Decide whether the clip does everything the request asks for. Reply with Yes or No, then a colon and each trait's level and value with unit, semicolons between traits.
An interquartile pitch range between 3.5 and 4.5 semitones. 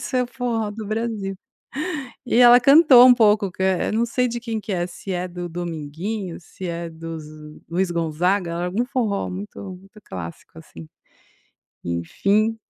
No: average, 5.0 semitones